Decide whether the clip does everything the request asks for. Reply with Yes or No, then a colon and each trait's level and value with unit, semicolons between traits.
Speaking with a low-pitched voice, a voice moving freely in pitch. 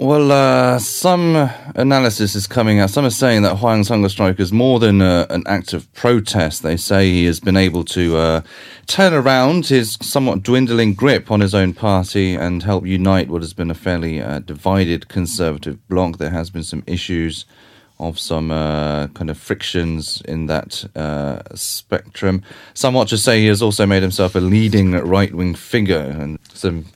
No: very low, 95 Hz; average, 5.0 semitones